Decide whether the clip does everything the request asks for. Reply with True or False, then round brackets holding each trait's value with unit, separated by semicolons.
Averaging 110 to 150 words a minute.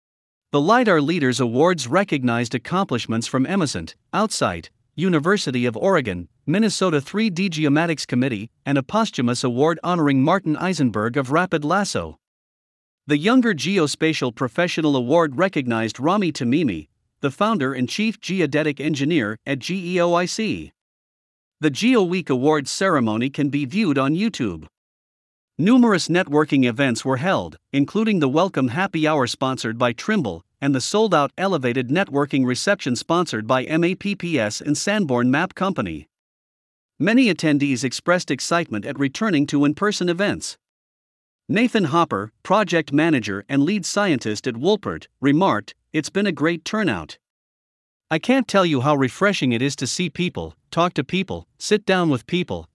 True (140 wpm)